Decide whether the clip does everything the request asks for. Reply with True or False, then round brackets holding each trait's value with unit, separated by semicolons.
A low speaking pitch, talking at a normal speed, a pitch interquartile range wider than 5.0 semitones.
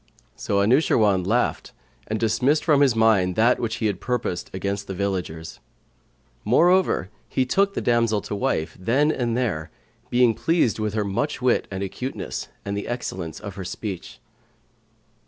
False (110 Hz; 155 wpm; 4.1 semitones)